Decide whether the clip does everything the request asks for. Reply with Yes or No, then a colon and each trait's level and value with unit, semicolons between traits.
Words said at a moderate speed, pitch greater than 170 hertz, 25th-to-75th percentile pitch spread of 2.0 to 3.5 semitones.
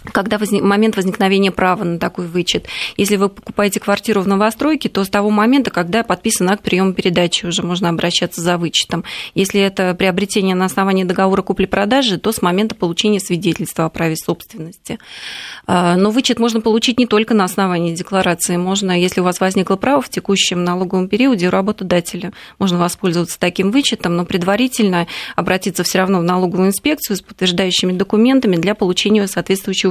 No: fast, 165 wpm; high, 190 Hz; narrow, 2.6 semitones